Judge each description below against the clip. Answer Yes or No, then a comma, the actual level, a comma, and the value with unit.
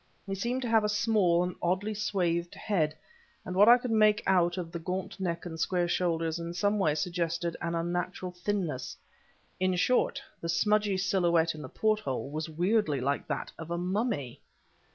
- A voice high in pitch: No, medium, 180 Hz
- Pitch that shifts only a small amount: No, average, 3.5 semitones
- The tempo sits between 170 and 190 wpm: Yes, average, 180 wpm